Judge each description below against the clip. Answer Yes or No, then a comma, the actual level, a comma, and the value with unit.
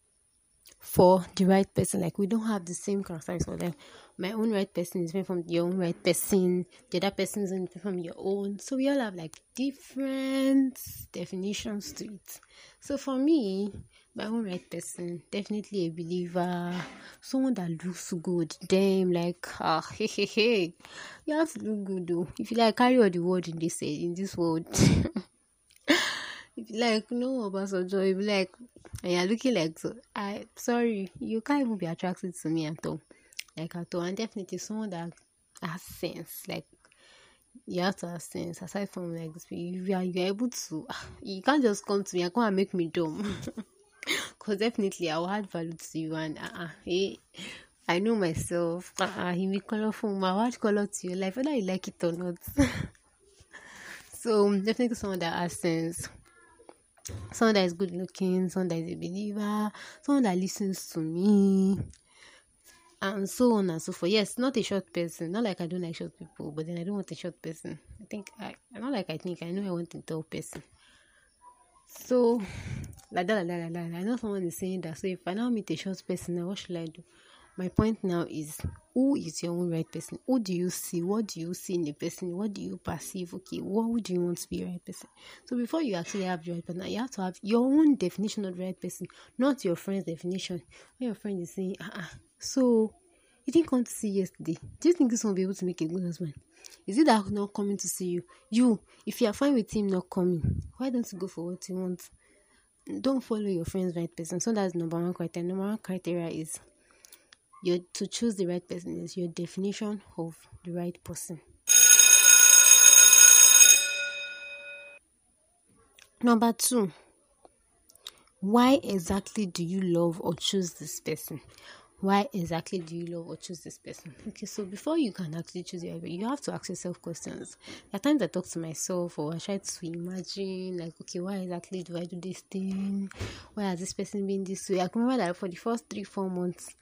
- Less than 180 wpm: No, fast, 205 wpm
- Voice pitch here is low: No, high, 190 Hz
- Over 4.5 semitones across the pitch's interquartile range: No, average, 4.0 semitones